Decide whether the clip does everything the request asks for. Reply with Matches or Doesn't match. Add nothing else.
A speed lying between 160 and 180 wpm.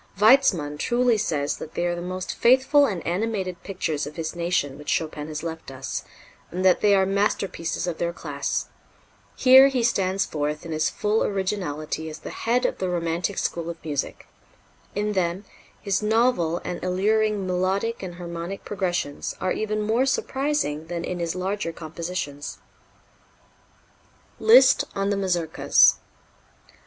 Doesn't match